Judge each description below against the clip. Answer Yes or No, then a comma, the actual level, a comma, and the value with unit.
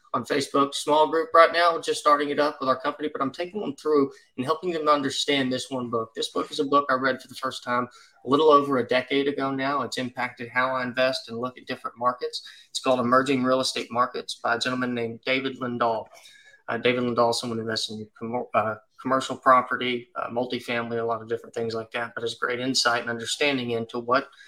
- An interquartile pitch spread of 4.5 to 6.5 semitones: No, average, 3.1 semitones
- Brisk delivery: Yes, fast, 225 wpm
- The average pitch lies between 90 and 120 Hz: No, low, 130 Hz